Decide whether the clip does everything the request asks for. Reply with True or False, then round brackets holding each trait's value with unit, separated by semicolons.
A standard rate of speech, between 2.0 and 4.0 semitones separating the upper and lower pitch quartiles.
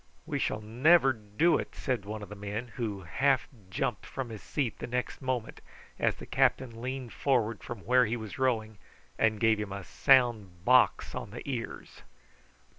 True (180 wpm; 3.3 semitones)